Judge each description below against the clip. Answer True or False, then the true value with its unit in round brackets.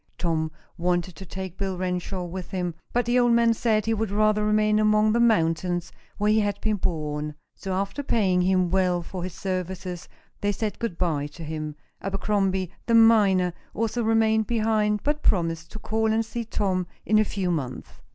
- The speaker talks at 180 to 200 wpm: True (185 wpm)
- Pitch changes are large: False (3.4 semitones)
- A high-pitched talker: True (195 Hz)